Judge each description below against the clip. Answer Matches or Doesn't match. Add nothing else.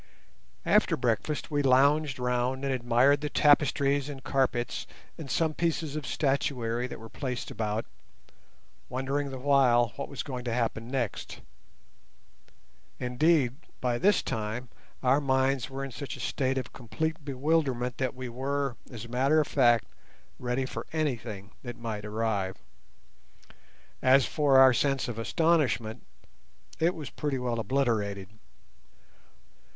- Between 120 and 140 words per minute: Matches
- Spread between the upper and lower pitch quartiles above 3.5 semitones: Doesn't match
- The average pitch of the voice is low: Matches